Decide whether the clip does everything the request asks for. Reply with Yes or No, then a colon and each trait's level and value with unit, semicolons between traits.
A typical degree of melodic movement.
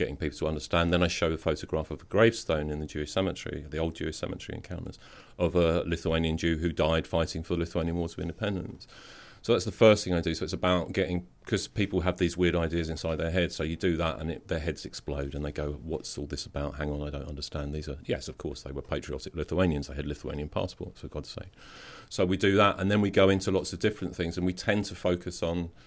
Yes: average, 3.1 semitones